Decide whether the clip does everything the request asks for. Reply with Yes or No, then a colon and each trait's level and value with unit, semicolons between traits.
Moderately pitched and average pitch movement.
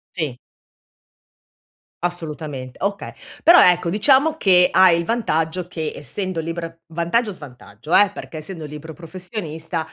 Yes: medium, 170 Hz; average, 3.1 semitones